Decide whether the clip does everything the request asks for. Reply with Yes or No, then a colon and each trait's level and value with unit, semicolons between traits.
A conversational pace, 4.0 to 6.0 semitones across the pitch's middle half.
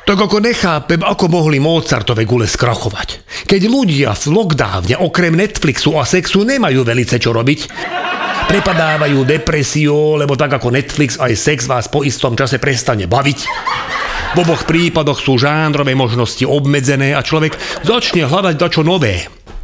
Yes: average, 145 wpm; average, 4.6 semitones